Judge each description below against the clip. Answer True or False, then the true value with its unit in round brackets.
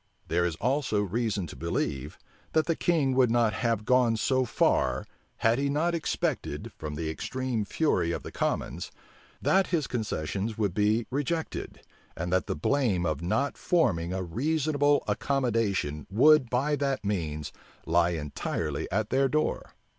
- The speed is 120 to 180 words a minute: True (155 wpm)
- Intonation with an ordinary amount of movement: False (7.8 semitones)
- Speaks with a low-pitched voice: True (115 Hz)